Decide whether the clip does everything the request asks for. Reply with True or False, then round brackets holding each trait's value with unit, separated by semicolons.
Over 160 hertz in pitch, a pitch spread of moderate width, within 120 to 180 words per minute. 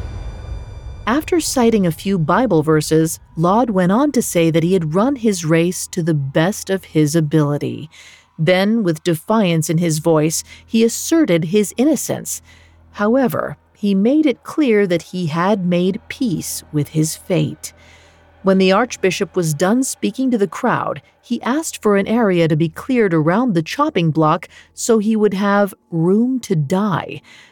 False (190 Hz; 5.7 semitones; 160 wpm)